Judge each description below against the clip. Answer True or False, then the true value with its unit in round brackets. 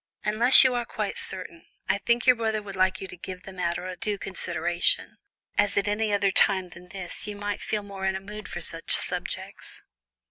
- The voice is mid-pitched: False (195 Hz)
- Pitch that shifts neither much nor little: False (2.2 semitones)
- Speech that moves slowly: False (205 wpm)